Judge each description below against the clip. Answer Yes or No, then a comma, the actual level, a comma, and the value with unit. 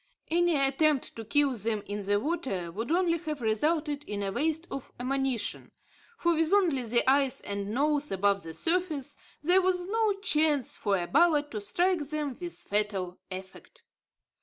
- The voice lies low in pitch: No, very high, 280 Hz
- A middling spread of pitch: No, wide, 7.6 semitones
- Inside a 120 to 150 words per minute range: No, average, 165 wpm